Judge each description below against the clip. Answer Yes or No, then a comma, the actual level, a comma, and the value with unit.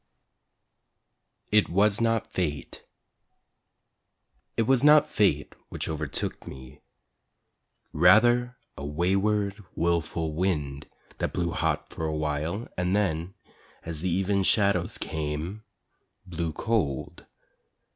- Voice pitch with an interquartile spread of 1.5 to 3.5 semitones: No, average, 5.1 semitones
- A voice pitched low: Yes, very low, 90 Hz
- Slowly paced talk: Yes, slow, 100 wpm